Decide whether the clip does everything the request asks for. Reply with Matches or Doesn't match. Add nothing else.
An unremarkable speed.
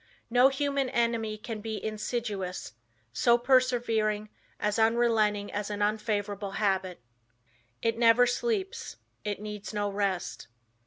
Doesn't match